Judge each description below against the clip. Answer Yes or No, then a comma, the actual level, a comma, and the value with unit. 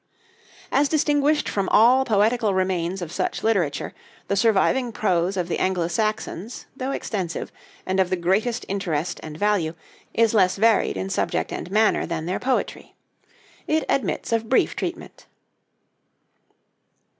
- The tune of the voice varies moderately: Yes, average, 4.2 semitones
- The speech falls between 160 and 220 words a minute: No, average, 140 wpm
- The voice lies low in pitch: No, high, 200 Hz